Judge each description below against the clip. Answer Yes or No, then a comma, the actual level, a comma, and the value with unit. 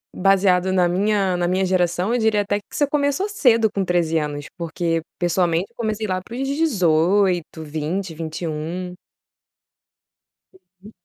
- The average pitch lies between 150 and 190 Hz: Yes, medium, 185 Hz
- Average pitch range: Yes, average, 3.4 semitones